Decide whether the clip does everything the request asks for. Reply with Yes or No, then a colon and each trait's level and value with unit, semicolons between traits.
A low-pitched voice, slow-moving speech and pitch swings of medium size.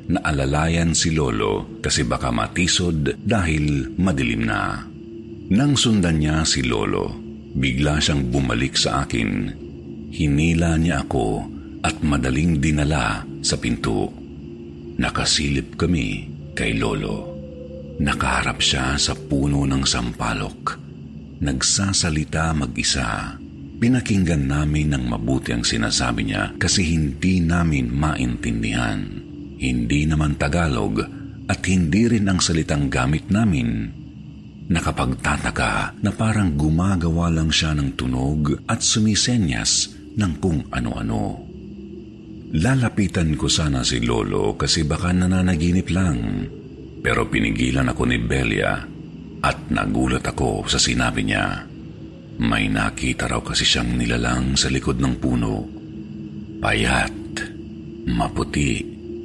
Yes: very low, 75 Hz; slow, 105 wpm; average, 4.4 semitones